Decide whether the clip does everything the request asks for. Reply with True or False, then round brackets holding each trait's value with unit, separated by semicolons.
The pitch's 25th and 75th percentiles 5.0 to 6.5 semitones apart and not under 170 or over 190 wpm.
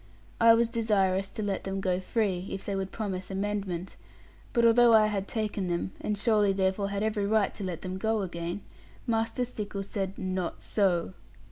False (2.4 semitones; 180 wpm)